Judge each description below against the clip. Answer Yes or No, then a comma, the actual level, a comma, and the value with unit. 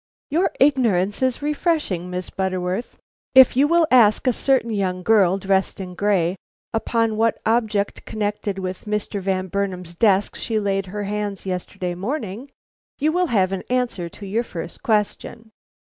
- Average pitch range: Yes, average, 3.9 semitones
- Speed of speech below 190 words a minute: Yes, average, 155 wpm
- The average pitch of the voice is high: Yes, high, 205 Hz